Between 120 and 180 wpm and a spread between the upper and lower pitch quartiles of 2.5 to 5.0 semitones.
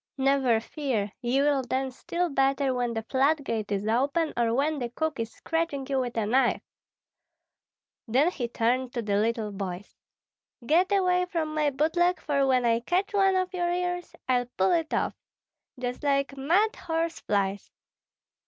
No: average, 170 wpm; wide, 5.5 semitones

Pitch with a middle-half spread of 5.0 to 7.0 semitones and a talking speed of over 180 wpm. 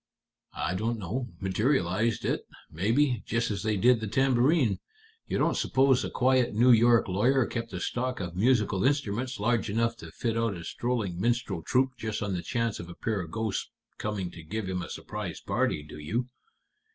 No: average, 4.3 semitones; average, 190 wpm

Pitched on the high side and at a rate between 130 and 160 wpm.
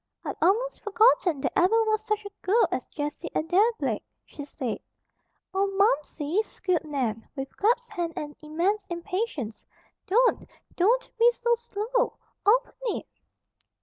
Yes: very high, 395 Hz; average, 140 wpm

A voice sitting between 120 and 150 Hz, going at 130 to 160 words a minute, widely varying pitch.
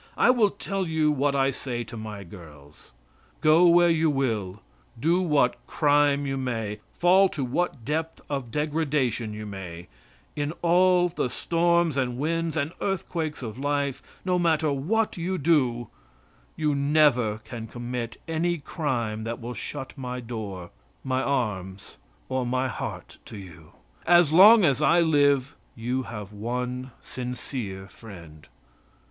Yes: low, 135 Hz; average, 145 wpm; wide, 5.8 semitones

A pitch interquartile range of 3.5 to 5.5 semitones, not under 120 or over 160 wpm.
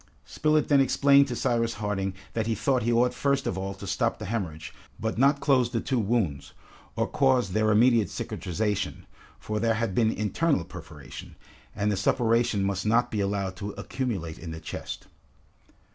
No: average, 3.9 semitones; average, 175 wpm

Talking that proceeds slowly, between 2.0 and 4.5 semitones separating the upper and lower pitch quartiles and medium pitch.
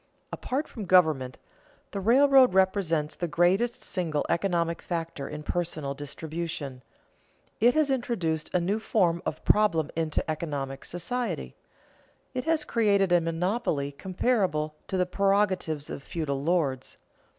No: slow, 130 wpm; average, 4.9 semitones; medium, 175 Hz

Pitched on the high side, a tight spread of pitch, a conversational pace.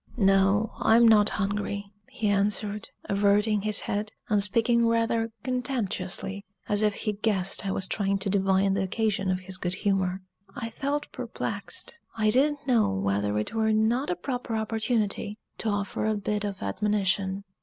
Yes: high, 205 Hz; narrow, 2.3 semitones; average, 160 wpm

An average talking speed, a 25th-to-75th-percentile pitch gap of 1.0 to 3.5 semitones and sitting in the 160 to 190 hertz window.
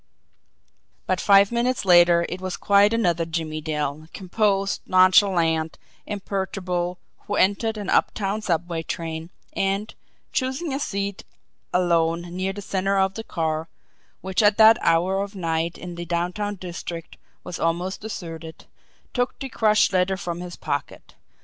Yes: average, 145 wpm; average, 3.0 semitones; medium, 185 Hz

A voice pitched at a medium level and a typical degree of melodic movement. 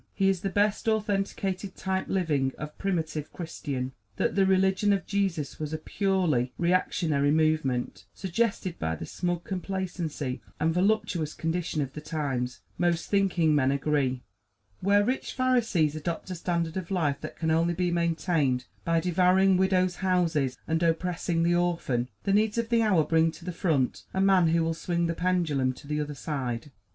Yes: medium, 170 Hz; average, 3.9 semitones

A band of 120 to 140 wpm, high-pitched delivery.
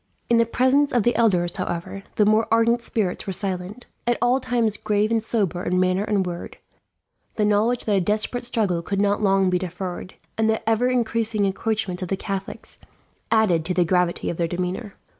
No: average, 195 wpm; high, 205 Hz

